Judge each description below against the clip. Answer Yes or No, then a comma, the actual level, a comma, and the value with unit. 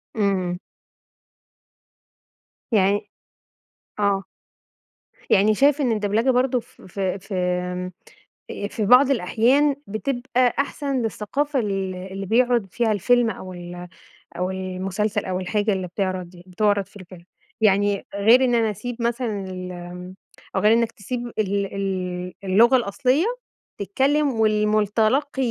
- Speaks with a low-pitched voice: No, high, 205 Hz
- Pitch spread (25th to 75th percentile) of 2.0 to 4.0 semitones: No, average, 4.4 semitones